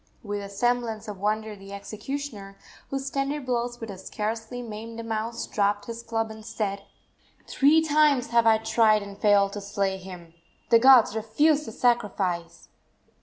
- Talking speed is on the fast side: No, average, 165 wpm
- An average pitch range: Yes, average, 3.1 semitones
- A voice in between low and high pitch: No, high, 220 Hz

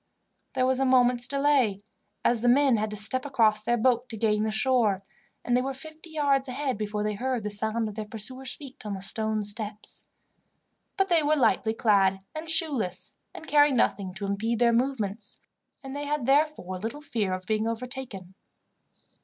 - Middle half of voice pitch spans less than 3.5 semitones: No, average, 4.1 semitones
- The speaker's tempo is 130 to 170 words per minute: No, average, 185 wpm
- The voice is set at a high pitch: Yes, high, 235 Hz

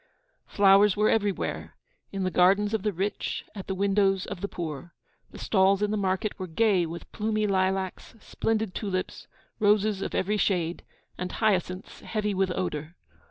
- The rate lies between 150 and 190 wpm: Yes, average, 160 wpm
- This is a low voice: No, high, 195 Hz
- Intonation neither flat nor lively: No, narrow, 2.2 semitones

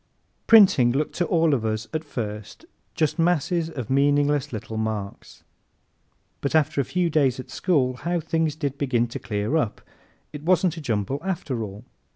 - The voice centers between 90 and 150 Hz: Yes, medium, 140 Hz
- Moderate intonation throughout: No, wide, 5.7 semitones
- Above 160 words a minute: Yes, average, 170 wpm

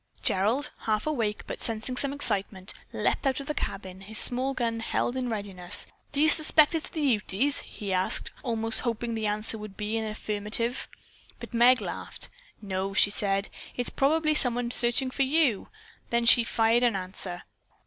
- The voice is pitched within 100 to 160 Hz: No, high, 230 Hz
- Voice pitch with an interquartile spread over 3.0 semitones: Yes, average, 3.9 semitones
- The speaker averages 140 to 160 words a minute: No, average, 180 wpm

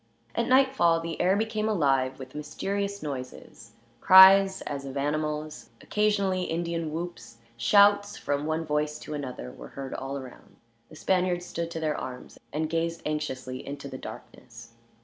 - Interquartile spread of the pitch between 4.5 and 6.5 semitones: Yes, average, 5.3 semitones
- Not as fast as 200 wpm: Yes, average, 150 wpm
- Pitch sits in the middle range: Yes, medium, 155 Hz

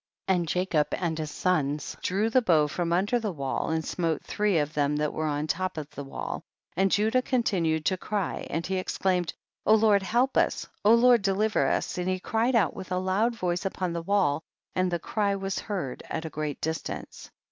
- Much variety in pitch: No, average, 4.3 semitones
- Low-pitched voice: No, medium, 185 Hz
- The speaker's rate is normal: No, fast, 210 wpm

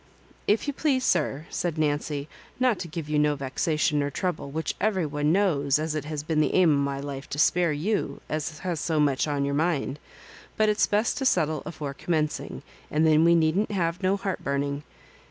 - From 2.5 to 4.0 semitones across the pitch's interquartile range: Yes, average, 3.4 semitones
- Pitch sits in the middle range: Yes, medium, 155 Hz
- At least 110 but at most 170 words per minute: No, fast, 205 wpm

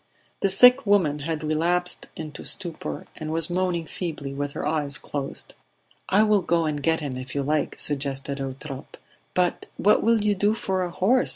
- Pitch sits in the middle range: Yes, medium, 160 Hz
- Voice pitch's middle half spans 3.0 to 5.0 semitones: Yes, average, 4.5 semitones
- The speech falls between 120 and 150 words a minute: No, average, 180 wpm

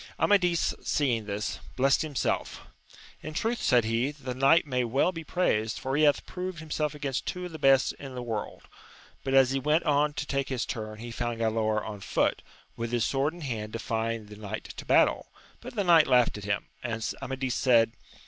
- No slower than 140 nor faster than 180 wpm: No, fast, 205 wpm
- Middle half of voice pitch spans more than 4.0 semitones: Yes, average, 4.8 semitones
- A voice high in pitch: No, low, 130 Hz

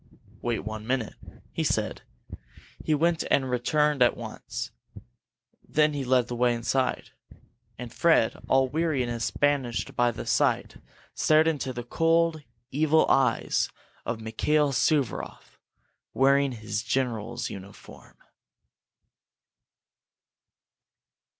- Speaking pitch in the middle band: No, low, 130 Hz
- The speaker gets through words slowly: Yes, slow, 105 wpm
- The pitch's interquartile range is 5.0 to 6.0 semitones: No, average, 4.0 semitones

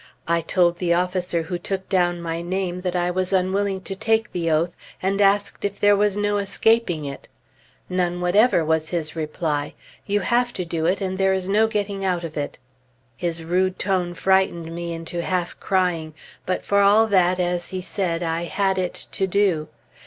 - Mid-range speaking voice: Yes, medium, 180 Hz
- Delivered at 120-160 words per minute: No, average, 190 wpm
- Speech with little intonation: Yes, narrow, 2.3 semitones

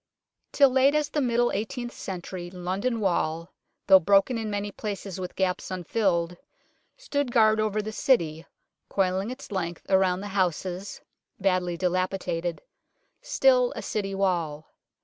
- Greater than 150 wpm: No, average, 140 wpm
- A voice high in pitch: Yes, high, 195 Hz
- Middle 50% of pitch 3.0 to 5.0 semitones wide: Yes, average, 4.0 semitones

